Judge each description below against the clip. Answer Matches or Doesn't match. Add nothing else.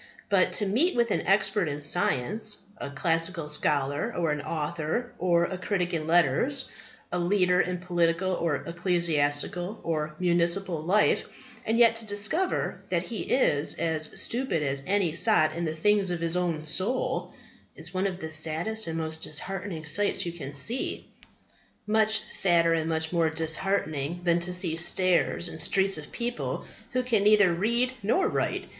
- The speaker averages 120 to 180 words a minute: Matches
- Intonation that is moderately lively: Matches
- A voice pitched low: Doesn't match